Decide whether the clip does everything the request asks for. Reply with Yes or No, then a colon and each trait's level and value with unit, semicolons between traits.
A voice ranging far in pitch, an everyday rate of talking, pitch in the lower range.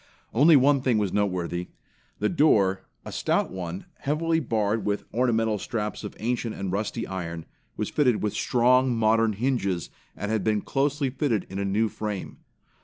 No: average, 4.3 semitones; average, 160 wpm; low, 110 Hz